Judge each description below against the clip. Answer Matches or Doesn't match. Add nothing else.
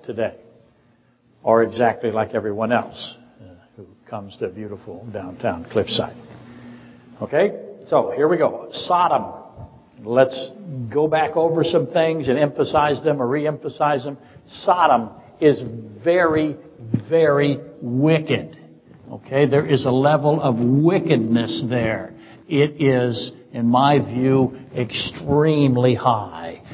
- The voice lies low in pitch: Matches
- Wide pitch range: Doesn't match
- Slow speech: Matches